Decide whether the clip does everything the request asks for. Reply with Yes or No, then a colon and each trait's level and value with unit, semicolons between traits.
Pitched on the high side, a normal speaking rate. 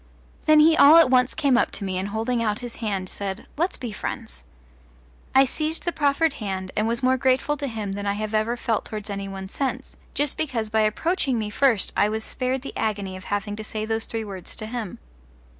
No: high, 225 Hz; fast, 225 wpm